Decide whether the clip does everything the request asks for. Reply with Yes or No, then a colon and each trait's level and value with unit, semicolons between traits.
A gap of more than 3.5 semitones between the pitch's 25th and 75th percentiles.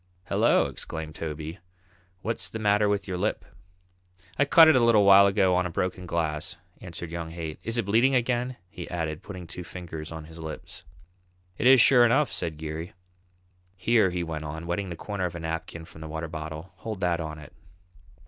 Yes: average, 4.2 semitones